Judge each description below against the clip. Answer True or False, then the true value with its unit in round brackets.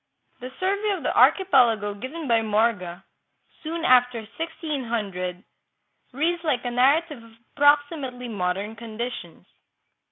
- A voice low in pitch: False (245 Hz)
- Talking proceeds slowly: True (115 wpm)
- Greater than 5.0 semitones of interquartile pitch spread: True (5.5 semitones)